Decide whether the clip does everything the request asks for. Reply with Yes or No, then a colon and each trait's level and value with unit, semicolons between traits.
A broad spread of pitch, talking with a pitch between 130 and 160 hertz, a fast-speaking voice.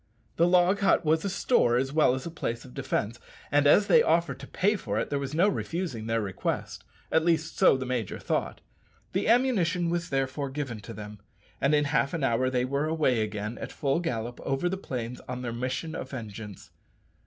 Yes: wide, 5.8 semitones; medium, 140 Hz; fast, 210 wpm